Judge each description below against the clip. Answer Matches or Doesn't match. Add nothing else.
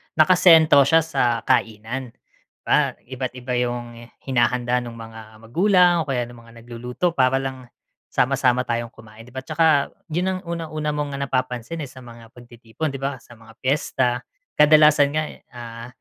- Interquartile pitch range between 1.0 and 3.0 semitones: Doesn't match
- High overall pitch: Doesn't match